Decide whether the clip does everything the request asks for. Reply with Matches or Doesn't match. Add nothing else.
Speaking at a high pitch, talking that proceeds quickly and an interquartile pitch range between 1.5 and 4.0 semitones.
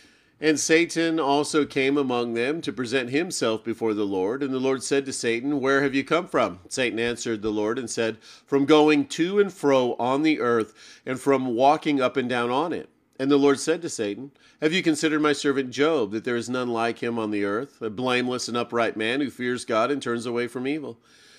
Doesn't match